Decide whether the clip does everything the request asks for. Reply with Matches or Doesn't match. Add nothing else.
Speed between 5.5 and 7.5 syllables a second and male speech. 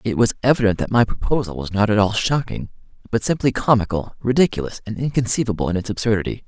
Matches